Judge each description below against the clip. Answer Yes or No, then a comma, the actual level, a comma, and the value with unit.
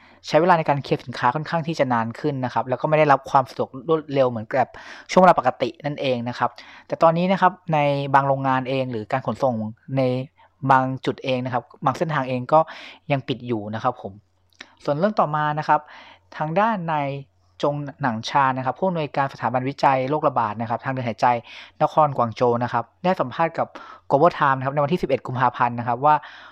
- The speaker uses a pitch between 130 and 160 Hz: Yes, low, 135 Hz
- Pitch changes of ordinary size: Yes, average, 3.7 semitones